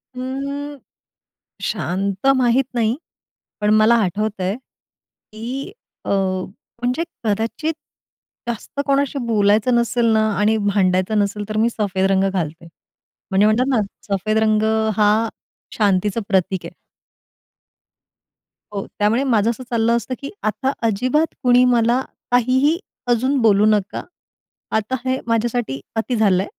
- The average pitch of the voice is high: Yes, high, 220 Hz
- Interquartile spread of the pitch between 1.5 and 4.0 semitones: Yes, average, 3.6 semitones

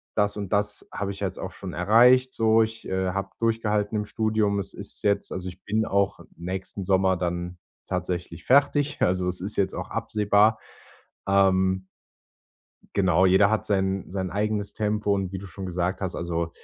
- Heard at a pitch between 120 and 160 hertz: No, low, 100 Hz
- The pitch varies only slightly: Yes, narrow, 2.2 semitones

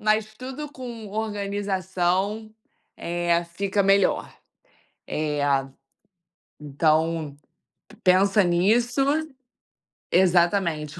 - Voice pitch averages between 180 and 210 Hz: Yes, high, 190 Hz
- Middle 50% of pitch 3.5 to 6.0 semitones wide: Yes, average, 3.9 semitones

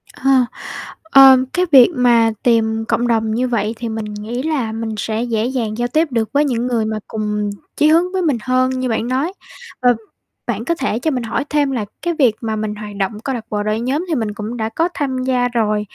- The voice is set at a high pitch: Yes, high, 240 Hz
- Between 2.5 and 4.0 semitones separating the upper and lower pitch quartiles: Yes, average, 3.3 semitones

